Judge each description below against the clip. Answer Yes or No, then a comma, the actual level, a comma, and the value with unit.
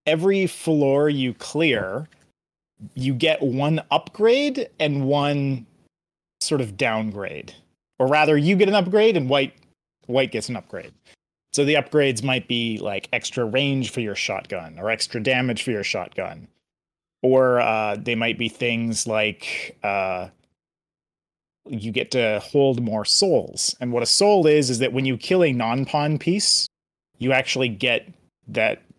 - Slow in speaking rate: No, average, 155 wpm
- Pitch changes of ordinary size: Yes, average, 4.4 semitones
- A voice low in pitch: Yes, low, 130 Hz